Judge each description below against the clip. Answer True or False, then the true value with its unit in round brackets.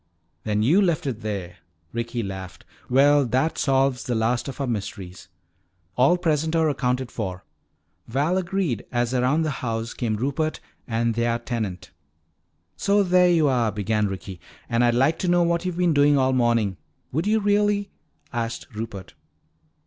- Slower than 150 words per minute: False (165 wpm)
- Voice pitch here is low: True (125 Hz)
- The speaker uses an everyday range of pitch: False (5.9 semitones)